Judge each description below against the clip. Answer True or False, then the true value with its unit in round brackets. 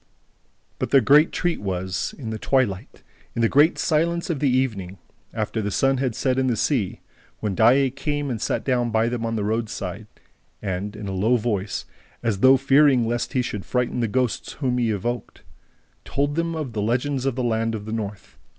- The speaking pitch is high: False (120 Hz)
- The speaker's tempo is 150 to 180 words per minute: False (195 wpm)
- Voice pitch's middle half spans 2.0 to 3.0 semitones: False (4.1 semitones)